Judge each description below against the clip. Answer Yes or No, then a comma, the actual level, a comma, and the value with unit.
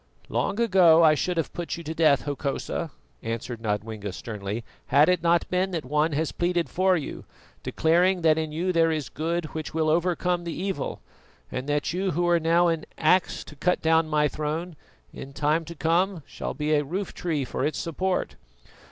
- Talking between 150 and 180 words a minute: No, average, 190 wpm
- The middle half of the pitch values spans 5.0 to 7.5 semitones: No, average, 2.7 semitones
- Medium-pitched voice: Yes, medium, 160 Hz